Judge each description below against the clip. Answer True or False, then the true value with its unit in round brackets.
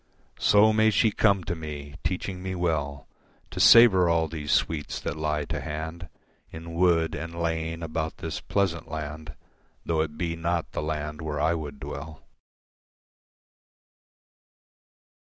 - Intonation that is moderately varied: False (2.2 semitones)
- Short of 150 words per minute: True (140 wpm)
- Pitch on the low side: True (80 Hz)